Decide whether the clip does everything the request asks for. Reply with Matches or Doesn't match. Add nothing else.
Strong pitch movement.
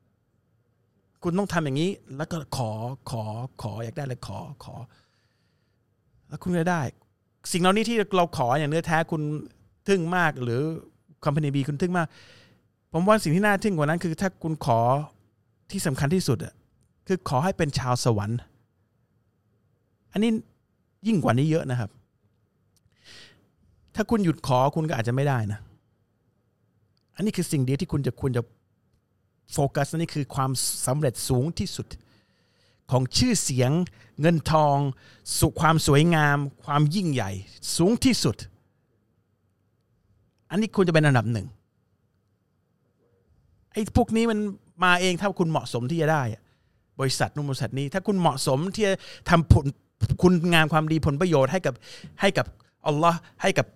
Matches